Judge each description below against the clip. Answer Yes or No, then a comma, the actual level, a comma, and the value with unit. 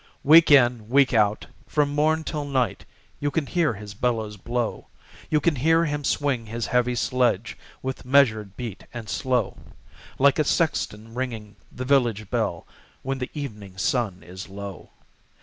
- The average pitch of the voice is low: Yes, low, 125 Hz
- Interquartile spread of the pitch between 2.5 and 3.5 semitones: No, average, 4.8 semitones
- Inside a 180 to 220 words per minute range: No, average, 155 wpm